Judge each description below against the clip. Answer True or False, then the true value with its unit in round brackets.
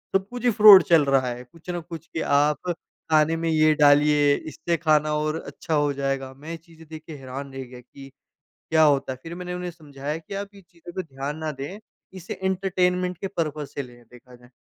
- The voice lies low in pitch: False (155 Hz)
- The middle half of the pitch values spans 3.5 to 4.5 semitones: True (4.0 semitones)